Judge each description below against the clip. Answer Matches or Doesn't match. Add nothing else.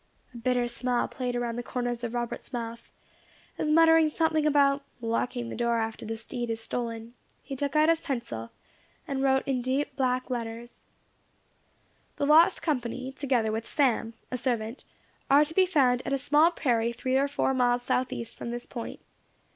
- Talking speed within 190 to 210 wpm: Doesn't match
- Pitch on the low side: Doesn't match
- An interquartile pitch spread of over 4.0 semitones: Doesn't match